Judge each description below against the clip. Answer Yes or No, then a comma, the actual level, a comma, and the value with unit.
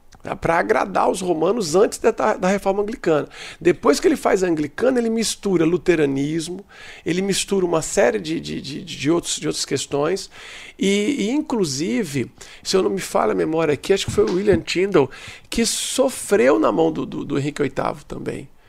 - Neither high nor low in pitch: No, high, 195 Hz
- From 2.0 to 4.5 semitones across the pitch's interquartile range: No, wide, 5.6 semitones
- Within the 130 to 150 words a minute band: No, fast, 185 wpm